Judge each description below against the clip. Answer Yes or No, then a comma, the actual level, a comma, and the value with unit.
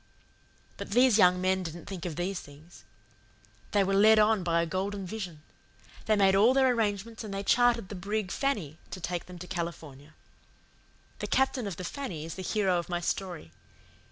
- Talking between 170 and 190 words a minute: Yes, average, 185 wpm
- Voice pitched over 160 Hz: Yes, high, 190 Hz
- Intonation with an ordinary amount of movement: Yes, average, 3.6 semitones